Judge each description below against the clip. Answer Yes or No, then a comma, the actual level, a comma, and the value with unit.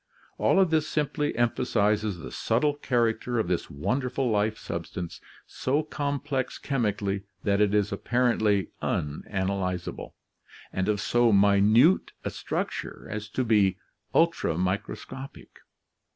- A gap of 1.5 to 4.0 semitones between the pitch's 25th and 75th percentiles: No, average, 4.8 semitones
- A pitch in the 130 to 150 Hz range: No, low, 110 Hz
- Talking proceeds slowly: Yes, slow, 125 wpm